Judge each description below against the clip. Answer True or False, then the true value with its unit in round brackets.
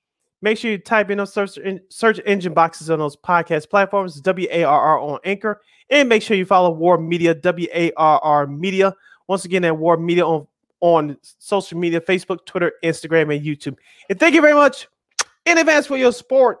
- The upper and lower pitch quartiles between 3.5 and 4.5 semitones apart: True (3.8 semitones)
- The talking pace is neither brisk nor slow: True (175 wpm)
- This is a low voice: False (185 Hz)